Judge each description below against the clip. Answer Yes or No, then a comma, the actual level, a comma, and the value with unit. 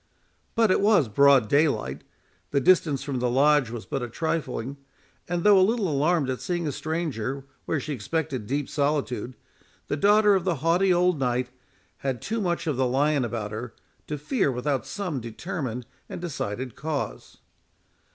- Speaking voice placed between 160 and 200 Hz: No, medium, 145 Hz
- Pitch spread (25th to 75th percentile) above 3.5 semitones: Yes, wide, 5.5 semitones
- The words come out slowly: No, average, 165 wpm